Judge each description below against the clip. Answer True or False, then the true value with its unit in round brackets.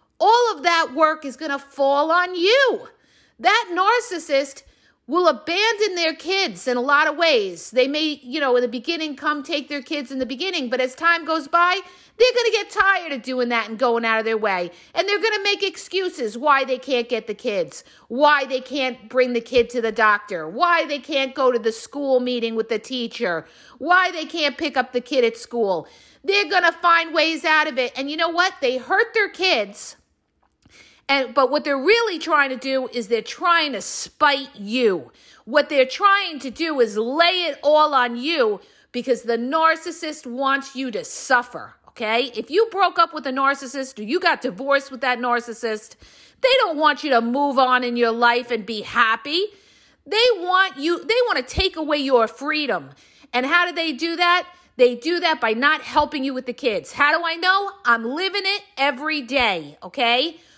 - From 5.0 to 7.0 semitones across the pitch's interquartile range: True (5.6 semitones)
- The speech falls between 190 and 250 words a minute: True (200 wpm)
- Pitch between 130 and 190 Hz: False (290 Hz)